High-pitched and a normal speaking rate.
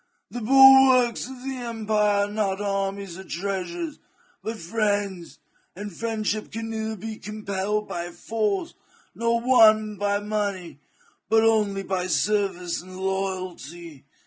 No: high, 210 Hz; slow, 120 wpm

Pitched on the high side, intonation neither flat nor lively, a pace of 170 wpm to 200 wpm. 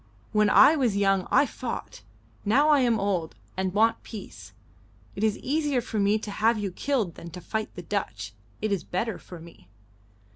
Yes: high, 210 Hz; average, 3.7 semitones; average, 185 wpm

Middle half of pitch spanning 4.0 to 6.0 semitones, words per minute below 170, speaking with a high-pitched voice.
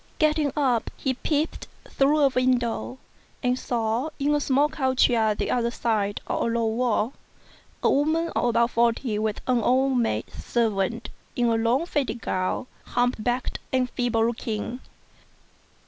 No: average, 2.8 semitones; average, 155 wpm; high, 245 Hz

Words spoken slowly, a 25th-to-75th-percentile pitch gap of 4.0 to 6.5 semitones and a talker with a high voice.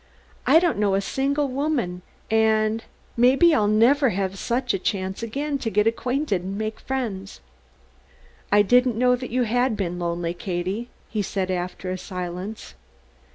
No: average, 160 wpm; average, 4.9 semitones; high, 220 Hz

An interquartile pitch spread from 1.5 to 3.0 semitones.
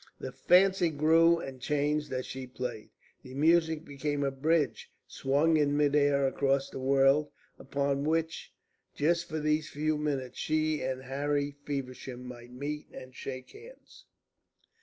Yes: narrow, 2.6 semitones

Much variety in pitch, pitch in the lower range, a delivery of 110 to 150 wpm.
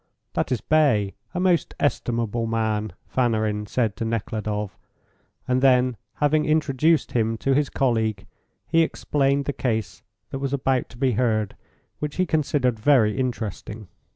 No: average, 4.3 semitones; low, 125 Hz; average, 145 wpm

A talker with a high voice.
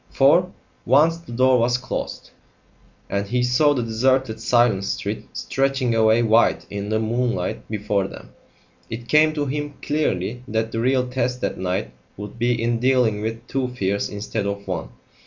No: low, 120 Hz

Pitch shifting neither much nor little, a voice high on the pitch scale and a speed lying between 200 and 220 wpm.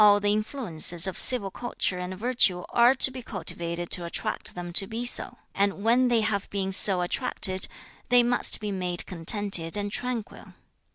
No: average, 4.7 semitones; high, 205 Hz; average, 170 wpm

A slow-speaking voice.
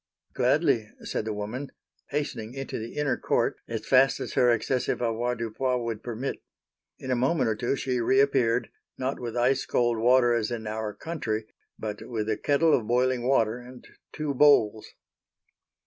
No: average, 165 wpm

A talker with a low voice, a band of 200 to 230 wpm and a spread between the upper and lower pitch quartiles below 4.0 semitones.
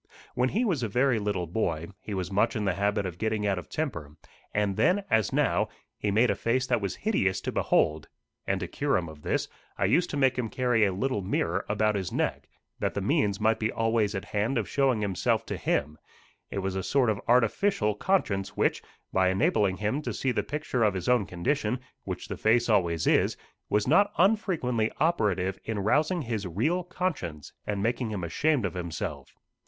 No: low, 110 Hz; fast, 205 wpm; average, 4.9 semitones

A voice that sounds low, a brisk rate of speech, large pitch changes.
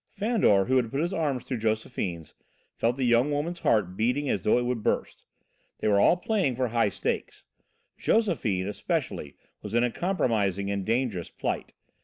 No: low, 120 Hz; average, 175 wpm; wide, 5.9 semitones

